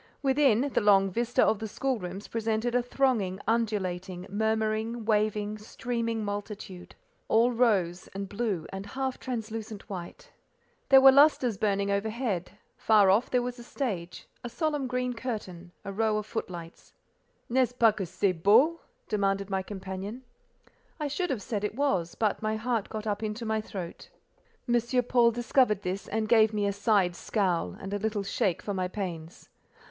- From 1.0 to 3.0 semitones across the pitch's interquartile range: No, average, 3.5 semitones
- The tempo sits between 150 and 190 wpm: Yes, average, 165 wpm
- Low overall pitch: No, high, 215 Hz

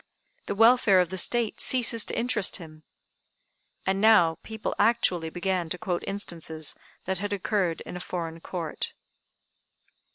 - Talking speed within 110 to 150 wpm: Yes, average, 140 wpm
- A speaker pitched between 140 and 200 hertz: Yes, high, 190 Hz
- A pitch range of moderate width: Yes, average, 4.4 semitones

